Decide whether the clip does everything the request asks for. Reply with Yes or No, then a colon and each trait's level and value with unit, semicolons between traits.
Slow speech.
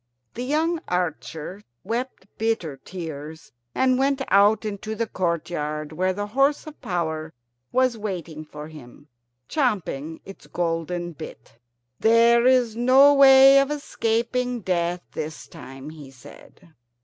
Yes: slow, 125 wpm